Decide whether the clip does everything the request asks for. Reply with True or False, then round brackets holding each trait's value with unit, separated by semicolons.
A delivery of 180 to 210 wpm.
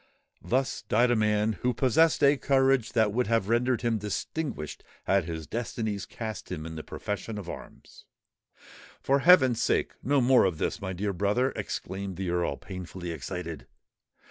False (165 wpm)